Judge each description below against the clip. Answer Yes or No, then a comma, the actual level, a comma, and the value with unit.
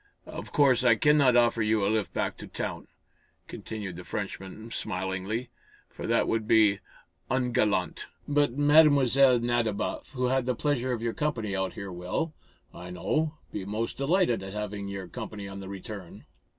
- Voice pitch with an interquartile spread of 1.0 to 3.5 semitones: No, average, 4.6 semitones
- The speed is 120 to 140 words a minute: No, average, 165 wpm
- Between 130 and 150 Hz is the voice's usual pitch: No, low, 115 Hz